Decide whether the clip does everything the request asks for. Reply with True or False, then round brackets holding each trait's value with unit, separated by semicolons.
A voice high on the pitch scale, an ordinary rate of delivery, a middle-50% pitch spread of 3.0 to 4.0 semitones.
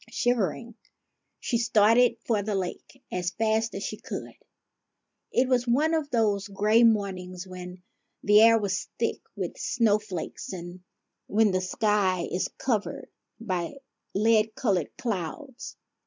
False (210 Hz; 130 wpm; 3.7 semitones)